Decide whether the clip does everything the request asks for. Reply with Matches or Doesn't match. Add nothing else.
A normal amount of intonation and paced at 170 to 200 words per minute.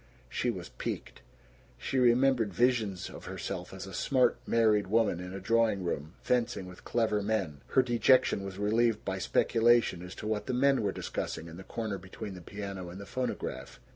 Matches